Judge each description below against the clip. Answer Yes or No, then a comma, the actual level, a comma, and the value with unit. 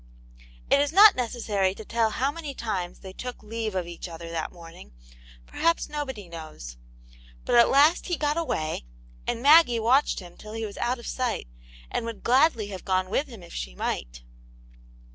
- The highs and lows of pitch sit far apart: Yes, wide, 7.3 semitones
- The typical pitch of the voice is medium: No, high, 225 Hz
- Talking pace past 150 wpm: Yes, average, 180 wpm